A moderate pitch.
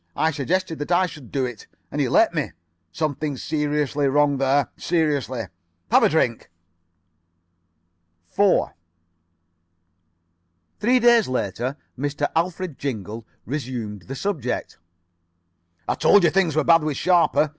Yes: medium, 145 Hz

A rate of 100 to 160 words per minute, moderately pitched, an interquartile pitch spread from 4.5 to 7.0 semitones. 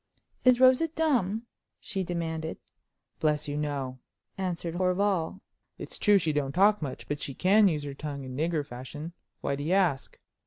No: average, 170 wpm; medium, 165 Hz; average, 5.1 semitones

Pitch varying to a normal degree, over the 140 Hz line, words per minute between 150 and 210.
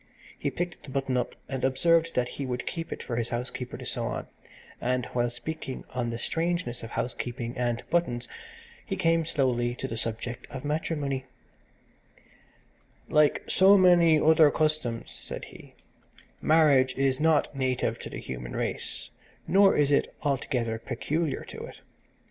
No: average, 4.7 semitones; low, 135 Hz; average, 155 wpm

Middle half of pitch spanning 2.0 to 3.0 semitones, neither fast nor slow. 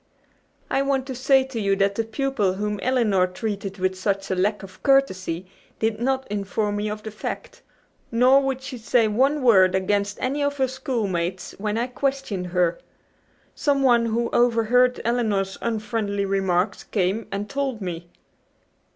No: average, 4.7 semitones; average, 160 wpm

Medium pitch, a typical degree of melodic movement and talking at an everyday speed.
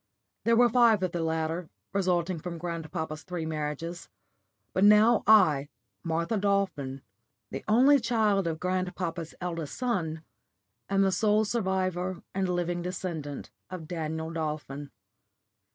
No: medium, 175 Hz; average, 3.7 semitones; slow, 125 wpm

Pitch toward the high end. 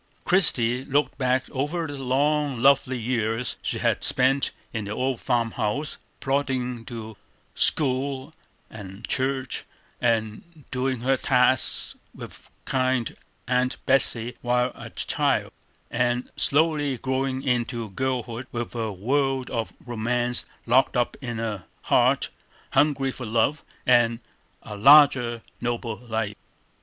No: low, 125 Hz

